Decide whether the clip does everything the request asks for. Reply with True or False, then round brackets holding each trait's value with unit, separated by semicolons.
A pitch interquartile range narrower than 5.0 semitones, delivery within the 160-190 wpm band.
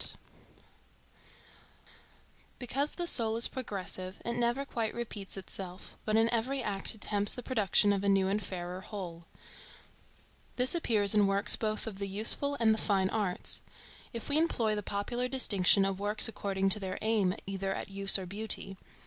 True (3.1 semitones; 165 wpm)